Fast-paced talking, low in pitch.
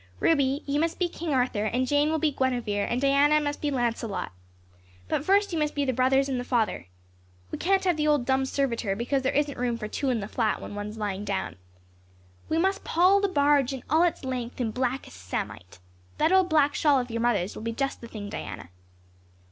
No: fast, 220 wpm; very high, 265 Hz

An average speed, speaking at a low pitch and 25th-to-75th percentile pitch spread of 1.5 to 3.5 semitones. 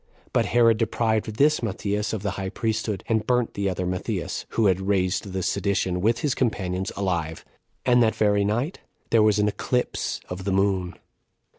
Yes: average, 175 wpm; low, 105 Hz; average, 3.0 semitones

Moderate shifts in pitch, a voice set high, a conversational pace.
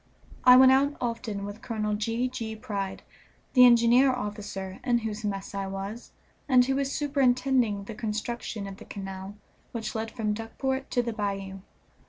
Yes: average, 3.6 semitones; high, 225 Hz; average, 165 wpm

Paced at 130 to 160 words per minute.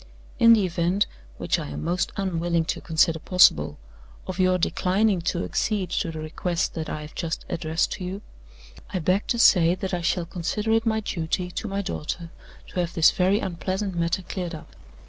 No: average, 190 wpm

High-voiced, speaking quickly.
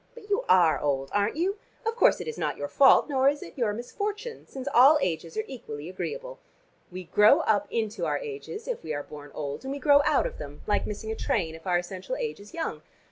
Yes: high, 230 Hz; fast, 235 wpm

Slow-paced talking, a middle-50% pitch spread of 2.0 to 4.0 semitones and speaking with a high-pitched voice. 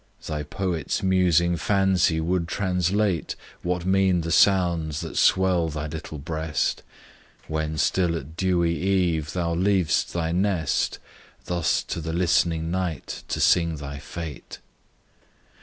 No: slow, 125 wpm; narrow, 2.4 semitones; very low, 85 Hz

